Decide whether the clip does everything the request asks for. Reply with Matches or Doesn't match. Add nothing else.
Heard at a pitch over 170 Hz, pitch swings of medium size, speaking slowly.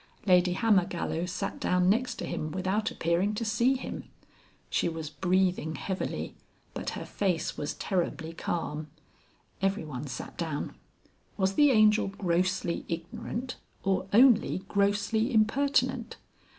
Matches